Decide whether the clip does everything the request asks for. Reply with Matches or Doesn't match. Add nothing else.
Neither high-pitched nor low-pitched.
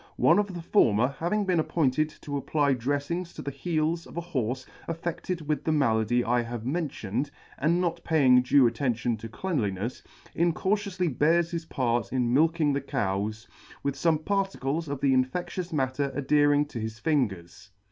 Matches